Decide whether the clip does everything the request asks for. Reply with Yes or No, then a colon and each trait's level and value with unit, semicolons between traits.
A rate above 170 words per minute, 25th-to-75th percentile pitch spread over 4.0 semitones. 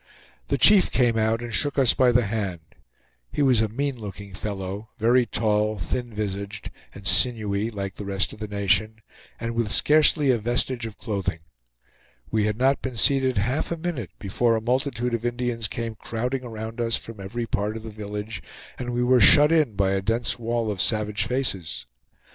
No: average, 190 wpm; average, 3.0 semitones